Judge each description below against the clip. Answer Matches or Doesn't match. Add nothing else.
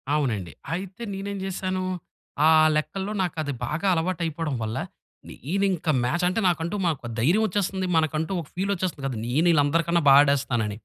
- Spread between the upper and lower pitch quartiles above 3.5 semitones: Matches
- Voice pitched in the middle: Matches